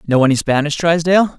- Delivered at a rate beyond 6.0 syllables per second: Yes, 6.4 syllables/s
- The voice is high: No, medium, 155 Hz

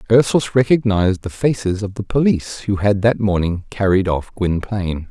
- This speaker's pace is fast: No, average, 165 wpm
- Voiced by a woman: No, male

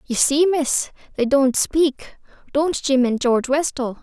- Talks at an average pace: Yes, average, 165 wpm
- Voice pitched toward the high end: Yes, very high, 275 Hz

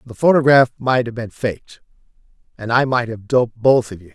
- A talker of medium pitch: No, low, 120 Hz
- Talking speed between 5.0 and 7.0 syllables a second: Yes, 5.7 syllables/s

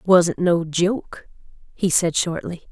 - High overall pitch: No, medium, 175 Hz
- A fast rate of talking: No, slow, 135 wpm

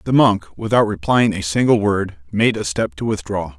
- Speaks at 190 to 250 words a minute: Yes, average, 200 wpm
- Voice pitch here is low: Yes, low, 100 Hz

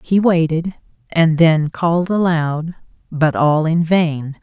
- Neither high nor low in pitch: Yes, medium, 165 Hz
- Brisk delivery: No, slow, 135 wpm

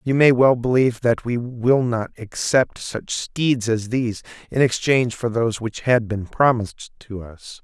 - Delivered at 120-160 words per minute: No, average, 180 wpm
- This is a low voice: Yes, low, 120 Hz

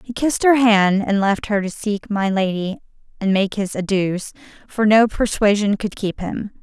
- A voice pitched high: Yes, high, 205 Hz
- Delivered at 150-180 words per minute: No, average, 190 wpm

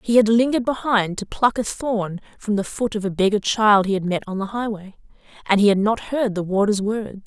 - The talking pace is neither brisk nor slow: No, fast, 240 wpm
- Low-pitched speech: No, high, 210 Hz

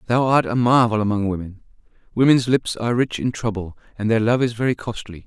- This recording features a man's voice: Yes, male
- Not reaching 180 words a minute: No, fast, 205 wpm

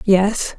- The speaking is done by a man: No, female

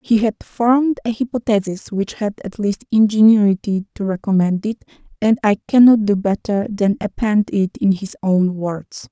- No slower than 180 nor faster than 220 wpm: No, average, 165 wpm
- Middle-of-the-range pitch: No, high, 210 Hz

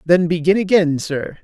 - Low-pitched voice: No, medium, 170 Hz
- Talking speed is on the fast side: No, average, 165 wpm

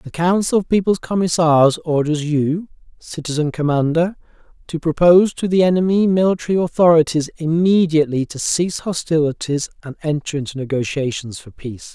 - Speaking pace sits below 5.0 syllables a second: No, 5.4 syllables/s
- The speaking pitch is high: No, medium, 160 Hz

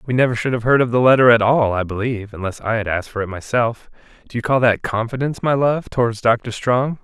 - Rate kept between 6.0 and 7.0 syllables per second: Yes, 6.3 syllables/s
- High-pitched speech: No, low, 120 Hz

